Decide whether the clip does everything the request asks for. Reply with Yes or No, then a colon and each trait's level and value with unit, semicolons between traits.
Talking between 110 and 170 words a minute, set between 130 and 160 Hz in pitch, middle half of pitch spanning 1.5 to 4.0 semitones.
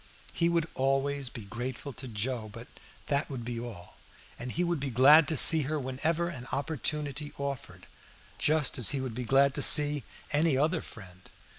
No: average, 180 wpm; low, 135 Hz; average, 3.5 semitones